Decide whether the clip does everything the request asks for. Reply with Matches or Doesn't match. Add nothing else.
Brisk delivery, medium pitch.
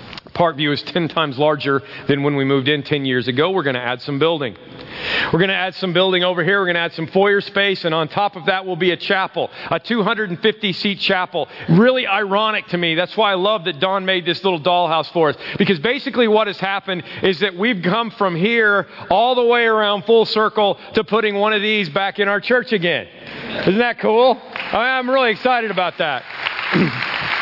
Doesn't match